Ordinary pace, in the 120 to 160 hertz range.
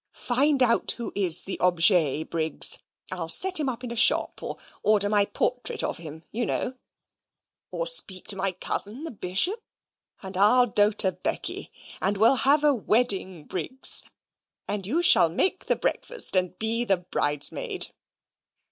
No: average, 155 wpm; high, 205 Hz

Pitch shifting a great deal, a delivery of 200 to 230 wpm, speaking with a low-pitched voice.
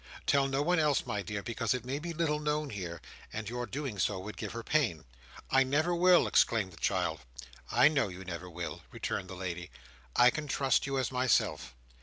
Yes: wide, 7.7 semitones; fast, 205 wpm; low, 120 Hz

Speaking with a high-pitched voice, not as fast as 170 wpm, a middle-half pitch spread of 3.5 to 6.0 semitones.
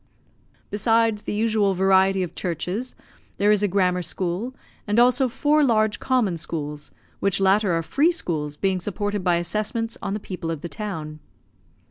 Yes: high, 195 Hz; average, 160 wpm; average, 3.9 semitones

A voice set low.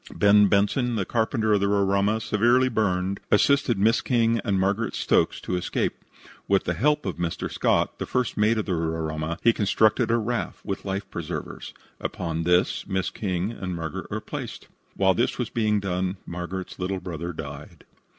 Yes: low, 100 Hz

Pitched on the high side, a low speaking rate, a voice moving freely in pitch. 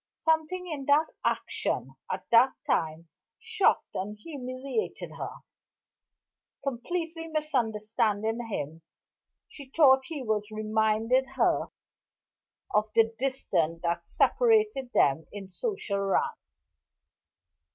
Yes: high, 245 Hz; slow, 100 wpm; wide, 6.7 semitones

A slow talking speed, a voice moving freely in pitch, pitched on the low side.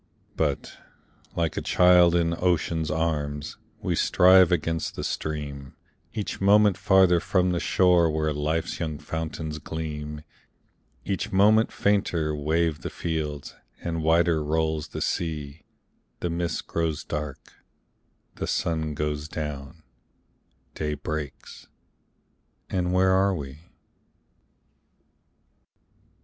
No: slow, 110 wpm; average, 2.7 semitones; very low, 80 Hz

